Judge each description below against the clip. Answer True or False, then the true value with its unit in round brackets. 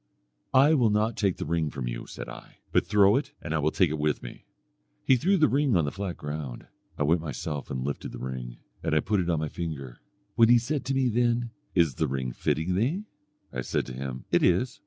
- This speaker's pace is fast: True (240 wpm)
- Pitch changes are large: True (8.6 semitones)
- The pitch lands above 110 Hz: False (85 Hz)